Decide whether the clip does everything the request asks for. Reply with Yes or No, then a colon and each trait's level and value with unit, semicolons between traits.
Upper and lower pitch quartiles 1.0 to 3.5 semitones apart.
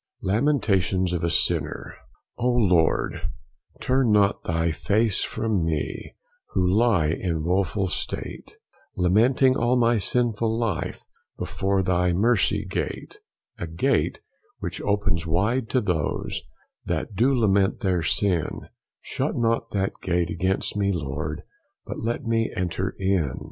No: average, 4.7 semitones